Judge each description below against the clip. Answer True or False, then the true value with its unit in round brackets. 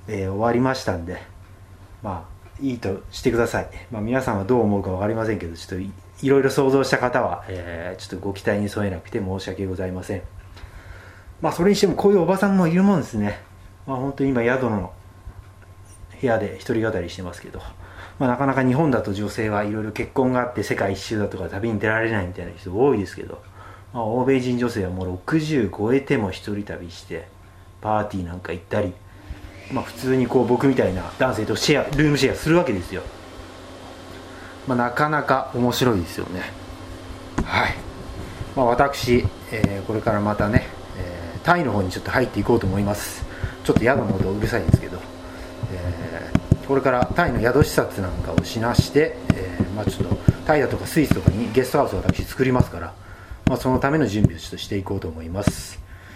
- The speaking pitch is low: True (100 Hz)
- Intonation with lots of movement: False (4.8 semitones)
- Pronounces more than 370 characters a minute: True (390 characters per minute)